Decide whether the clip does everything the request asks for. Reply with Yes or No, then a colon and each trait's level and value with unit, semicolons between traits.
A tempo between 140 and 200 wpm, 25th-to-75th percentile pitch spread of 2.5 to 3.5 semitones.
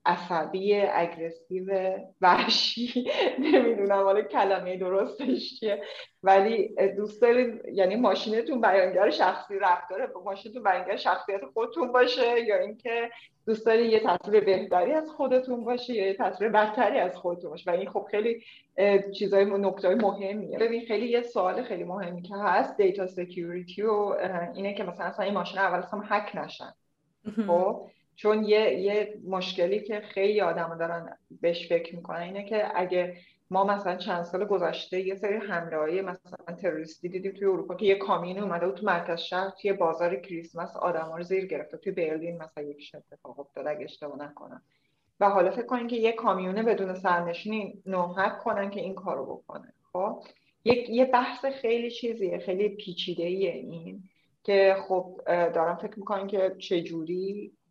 Yes: average, 150 wpm; average, 3.1 semitones